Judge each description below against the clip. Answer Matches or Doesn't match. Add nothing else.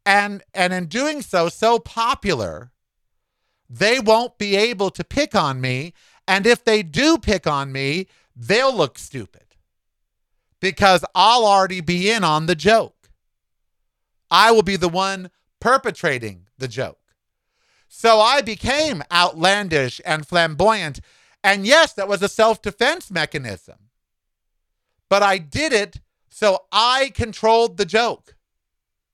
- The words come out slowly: Matches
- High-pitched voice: Matches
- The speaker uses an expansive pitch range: Matches